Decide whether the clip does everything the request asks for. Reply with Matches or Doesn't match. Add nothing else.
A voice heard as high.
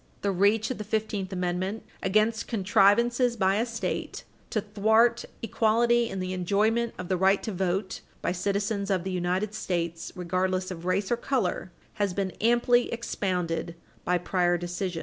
Matches